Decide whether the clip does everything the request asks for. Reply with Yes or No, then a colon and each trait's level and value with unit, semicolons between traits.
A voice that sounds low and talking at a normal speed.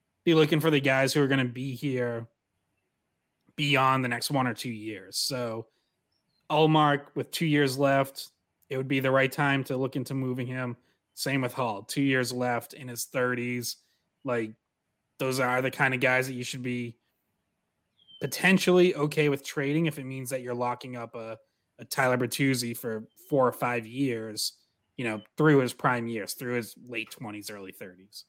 Yes: low, 130 Hz; average, 185 wpm